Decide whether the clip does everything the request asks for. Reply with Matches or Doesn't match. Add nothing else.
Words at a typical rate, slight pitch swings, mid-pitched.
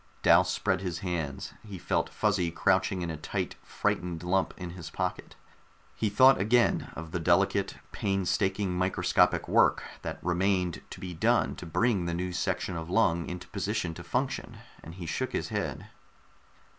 Doesn't match